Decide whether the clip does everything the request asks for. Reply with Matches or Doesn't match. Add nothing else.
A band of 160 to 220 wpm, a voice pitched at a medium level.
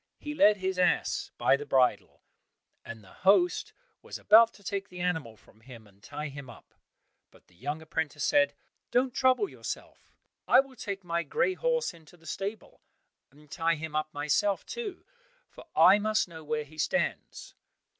Matches